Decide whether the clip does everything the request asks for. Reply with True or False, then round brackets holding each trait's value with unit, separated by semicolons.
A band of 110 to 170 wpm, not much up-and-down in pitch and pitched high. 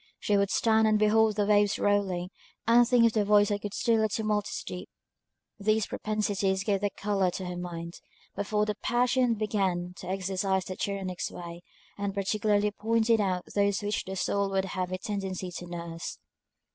False (180 wpm; 2.2 semitones; 200 Hz)